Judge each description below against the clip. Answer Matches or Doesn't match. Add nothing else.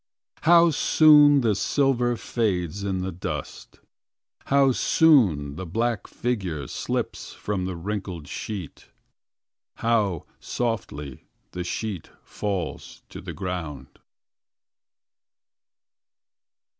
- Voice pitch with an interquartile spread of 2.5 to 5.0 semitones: Doesn't match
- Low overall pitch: Matches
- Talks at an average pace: Doesn't match